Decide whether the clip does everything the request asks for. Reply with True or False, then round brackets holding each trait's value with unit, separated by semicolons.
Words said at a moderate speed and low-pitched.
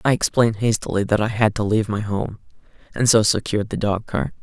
False (215 wpm; 105 Hz)